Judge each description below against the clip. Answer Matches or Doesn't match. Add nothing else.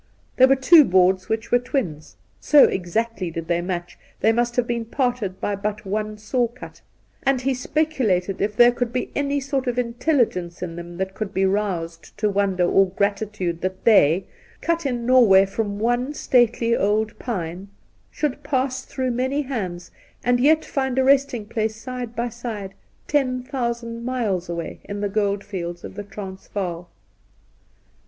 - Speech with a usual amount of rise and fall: Matches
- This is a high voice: Matches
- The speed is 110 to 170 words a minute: Matches